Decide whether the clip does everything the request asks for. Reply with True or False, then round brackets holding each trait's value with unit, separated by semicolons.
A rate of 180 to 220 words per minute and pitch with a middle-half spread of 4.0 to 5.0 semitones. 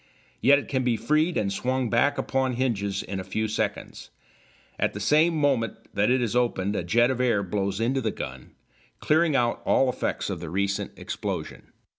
True (190 wpm; 4.7 semitones)